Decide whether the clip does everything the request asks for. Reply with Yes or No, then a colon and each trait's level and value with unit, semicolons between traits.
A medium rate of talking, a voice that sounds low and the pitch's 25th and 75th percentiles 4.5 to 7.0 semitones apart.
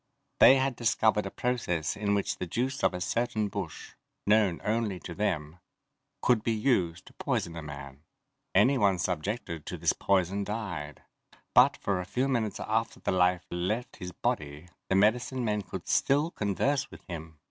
Yes: average, 170 wpm; low, 100 Hz; average, 4.9 semitones